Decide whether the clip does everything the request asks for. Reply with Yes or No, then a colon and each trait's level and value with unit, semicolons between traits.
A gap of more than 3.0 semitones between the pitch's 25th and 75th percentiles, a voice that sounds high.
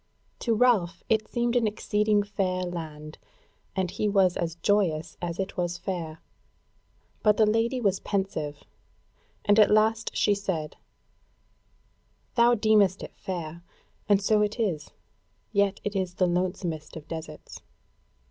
Yes: average, 3.6 semitones; high, 195 Hz